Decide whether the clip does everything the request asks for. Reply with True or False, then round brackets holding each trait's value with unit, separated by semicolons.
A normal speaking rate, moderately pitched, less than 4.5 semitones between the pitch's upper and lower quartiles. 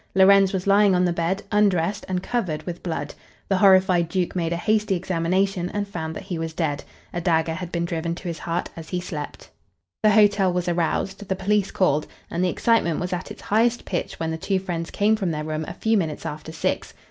False (220 wpm; 180 Hz; 2.9 semitones)